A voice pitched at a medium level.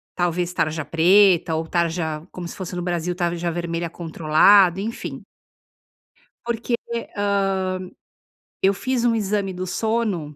Yes: medium, 180 Hz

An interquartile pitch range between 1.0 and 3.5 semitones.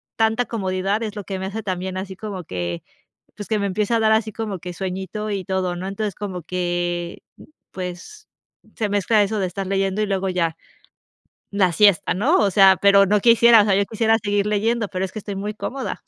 Yes: narrow, 2.4 semitones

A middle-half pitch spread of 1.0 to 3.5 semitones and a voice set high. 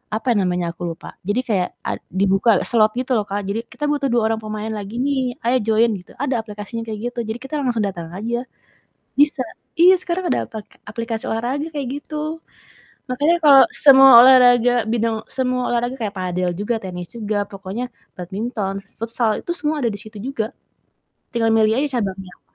No: average, 4.0 semitones; high, 230 Hz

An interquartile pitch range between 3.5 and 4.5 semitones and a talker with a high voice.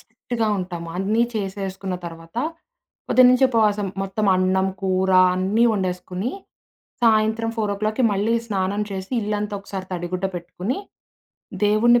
No: average, 2.7 semitones; high, 200 Hz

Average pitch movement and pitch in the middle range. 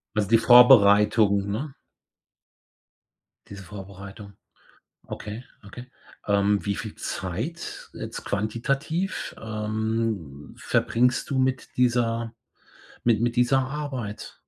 No: average, 3.5 semitones; low, 110 Hz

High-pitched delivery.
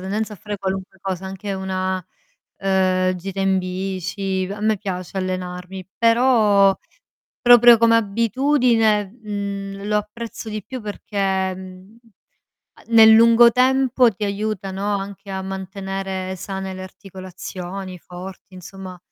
Yes: high, 195 Hz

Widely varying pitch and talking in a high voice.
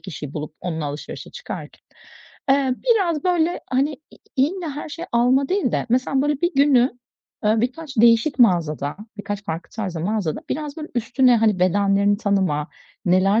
Yes: wide, 7.2 semitones; high, 235 Hz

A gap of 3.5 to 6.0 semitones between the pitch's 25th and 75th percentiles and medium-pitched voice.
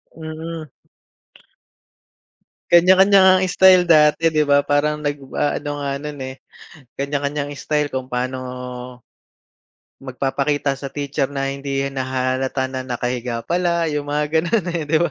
No: average, 2.8 semitones; medium, 145 Hz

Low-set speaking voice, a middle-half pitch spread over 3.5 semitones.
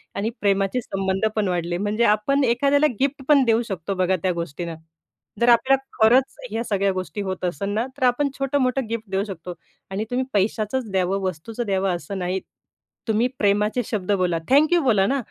No: high, 210 Hz; average, 4.6 semitones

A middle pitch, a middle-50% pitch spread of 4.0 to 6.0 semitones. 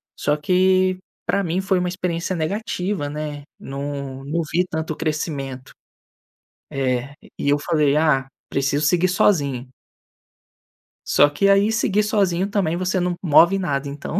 Yes: medium, 160 Hz; average, 4.5 semitones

